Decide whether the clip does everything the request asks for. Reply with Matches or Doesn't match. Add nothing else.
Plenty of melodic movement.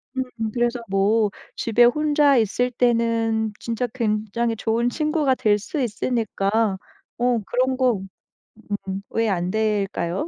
Doesn't match